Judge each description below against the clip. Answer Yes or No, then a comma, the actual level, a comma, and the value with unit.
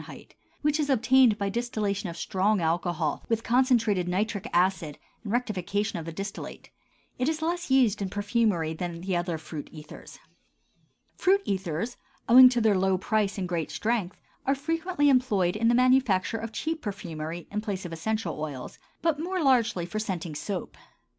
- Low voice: No, high, 205 Hz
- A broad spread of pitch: Yes, wide, 5.9 semitones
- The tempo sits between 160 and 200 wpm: Yes, average, 165 wpm